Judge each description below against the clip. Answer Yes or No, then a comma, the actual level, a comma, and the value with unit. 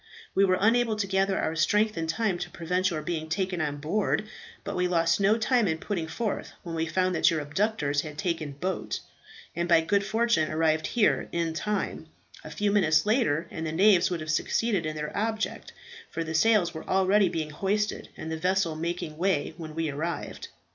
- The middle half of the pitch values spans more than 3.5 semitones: Yes, average, 4.2 semitones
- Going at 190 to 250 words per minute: Yes, average, 200 wpm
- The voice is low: No, medium, 175 Hz